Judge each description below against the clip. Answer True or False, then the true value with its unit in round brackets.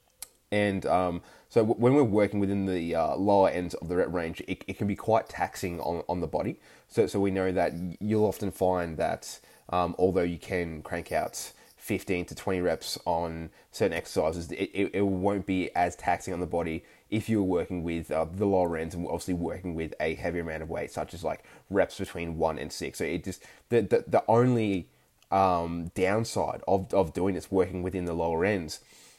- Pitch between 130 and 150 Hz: False (90 Hz)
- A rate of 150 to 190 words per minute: False (205 wpm)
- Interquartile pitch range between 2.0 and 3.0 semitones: True (2.5 semitones)